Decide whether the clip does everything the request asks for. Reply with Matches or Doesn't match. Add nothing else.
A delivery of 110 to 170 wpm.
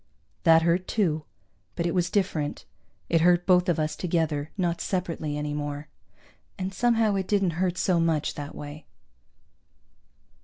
Matches